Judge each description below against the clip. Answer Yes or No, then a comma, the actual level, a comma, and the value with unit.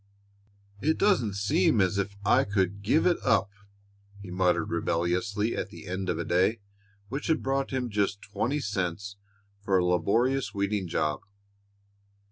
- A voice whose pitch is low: Yes, low, 100 Hz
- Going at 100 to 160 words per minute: Yes, average, 150 wpm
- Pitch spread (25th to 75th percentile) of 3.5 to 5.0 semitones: Yes, average, 4.1 semitones